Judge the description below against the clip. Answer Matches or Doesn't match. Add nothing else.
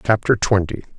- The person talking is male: Matches